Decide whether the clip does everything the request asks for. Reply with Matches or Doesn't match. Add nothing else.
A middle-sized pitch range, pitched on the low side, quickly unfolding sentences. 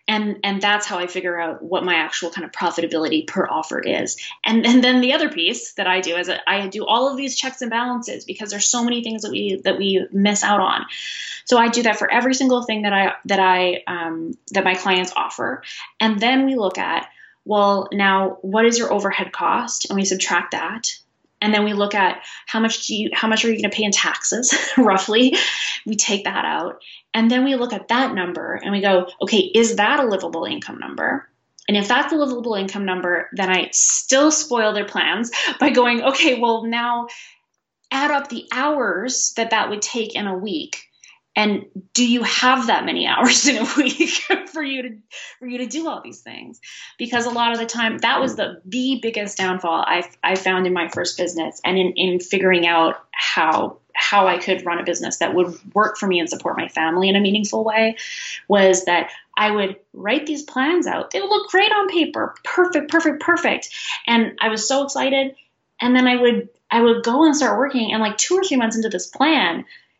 Doesn't match